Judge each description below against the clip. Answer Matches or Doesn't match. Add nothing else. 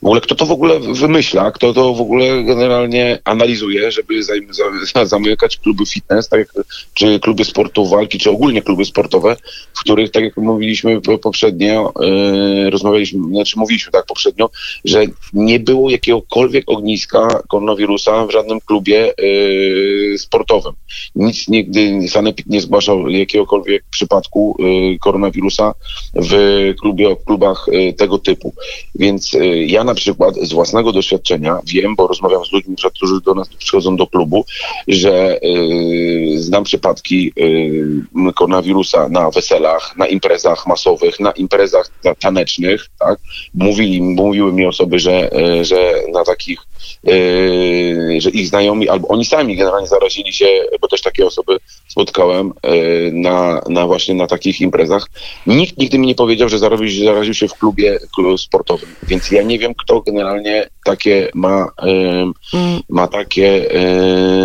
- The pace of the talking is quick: Doesn't match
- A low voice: Matches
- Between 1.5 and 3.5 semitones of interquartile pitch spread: Doesn't match